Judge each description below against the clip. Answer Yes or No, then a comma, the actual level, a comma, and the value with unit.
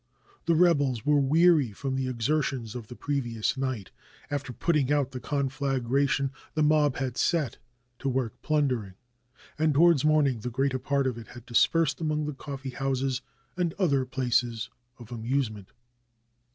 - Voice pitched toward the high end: No, low, 135 Hz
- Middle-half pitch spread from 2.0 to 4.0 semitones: Yes, average, 3.0 semitones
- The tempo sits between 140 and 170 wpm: Yes, average, 155 wpm